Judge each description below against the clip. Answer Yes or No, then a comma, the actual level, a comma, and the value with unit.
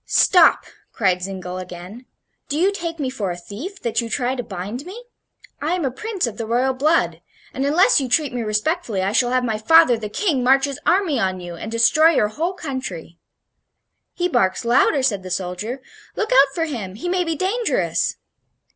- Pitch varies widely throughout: Yes, wide, 7.6 semitones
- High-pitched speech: Yes, very high, 255 Hz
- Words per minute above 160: Yes, average, 200 wpm